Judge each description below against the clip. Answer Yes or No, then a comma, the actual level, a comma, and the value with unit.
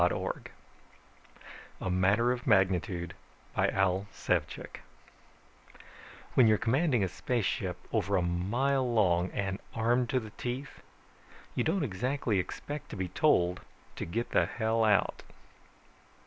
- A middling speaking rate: No, slow, 125 wpm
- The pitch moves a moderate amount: Yes, average, 5.0 semitones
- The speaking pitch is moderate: No, low, 110 Hz